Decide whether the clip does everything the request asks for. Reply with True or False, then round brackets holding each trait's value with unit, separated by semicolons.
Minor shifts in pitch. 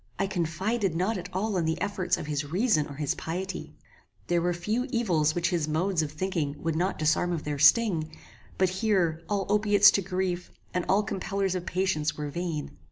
False (3.6 semitones)